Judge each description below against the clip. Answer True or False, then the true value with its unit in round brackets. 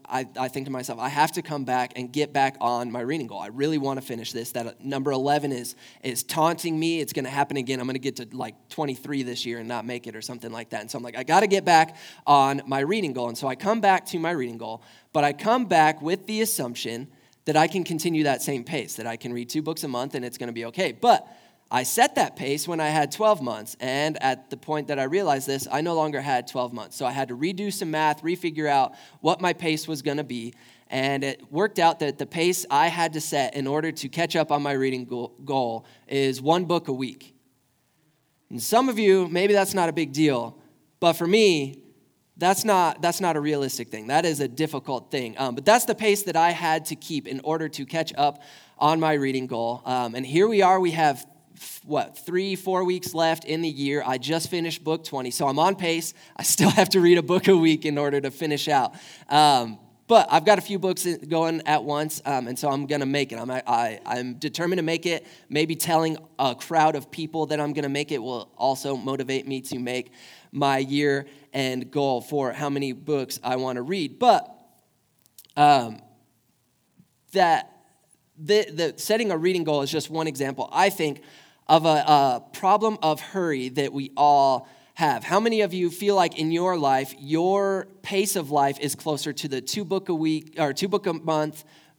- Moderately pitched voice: True (150 Hz)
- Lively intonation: False (3.9 semitones)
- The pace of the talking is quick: True (235 wpm)